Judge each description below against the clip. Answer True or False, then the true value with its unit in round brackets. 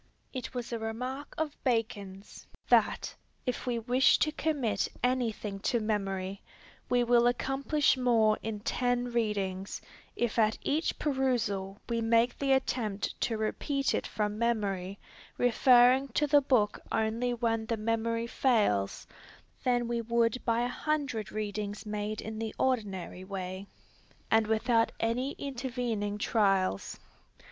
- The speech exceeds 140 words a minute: False (135 wpm)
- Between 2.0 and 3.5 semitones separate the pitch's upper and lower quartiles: True (2.9 semitones)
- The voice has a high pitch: True (230 Hz)